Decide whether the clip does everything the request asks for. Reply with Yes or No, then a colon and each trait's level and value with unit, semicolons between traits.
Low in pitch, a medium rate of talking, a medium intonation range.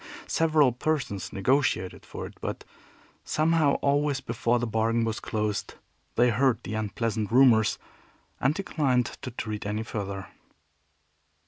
No: low, 120 Hz; slow, 125 wpm; average, 4.4 semitones